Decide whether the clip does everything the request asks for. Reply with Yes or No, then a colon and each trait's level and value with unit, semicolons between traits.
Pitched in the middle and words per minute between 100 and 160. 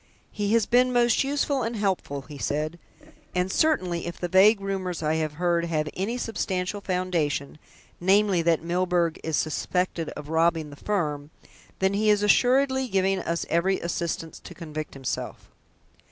Yes: medium, 180 Hz; average, 155 wpm